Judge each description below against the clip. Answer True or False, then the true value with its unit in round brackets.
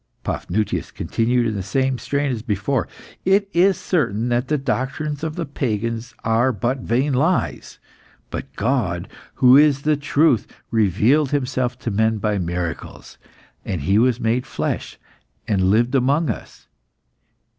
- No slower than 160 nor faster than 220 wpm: False (145 wpm)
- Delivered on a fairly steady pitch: False (4.5 semitones)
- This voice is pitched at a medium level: False (125 Hz)